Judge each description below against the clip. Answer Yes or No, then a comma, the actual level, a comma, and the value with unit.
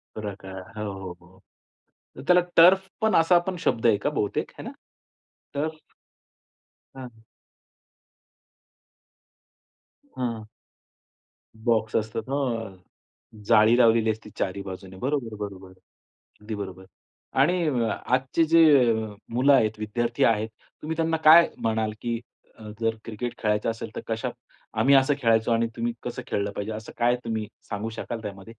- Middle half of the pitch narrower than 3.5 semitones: No, average, 3.8 semitones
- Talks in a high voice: No, low, 115 Hz